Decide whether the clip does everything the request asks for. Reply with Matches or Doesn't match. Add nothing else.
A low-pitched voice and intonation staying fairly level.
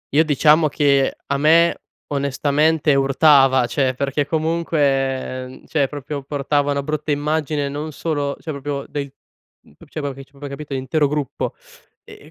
Doesn't match